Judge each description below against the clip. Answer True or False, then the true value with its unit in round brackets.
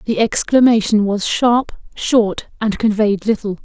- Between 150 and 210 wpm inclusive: False (130 wpm)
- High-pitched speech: True (215 Hz)